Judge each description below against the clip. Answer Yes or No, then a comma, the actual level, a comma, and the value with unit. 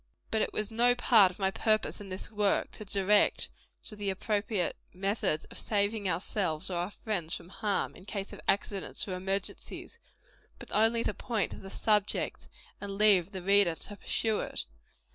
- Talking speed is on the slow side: No, average, 180 wpm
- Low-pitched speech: No, high, 200 Hz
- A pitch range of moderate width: No, narrow, 2.1 semitones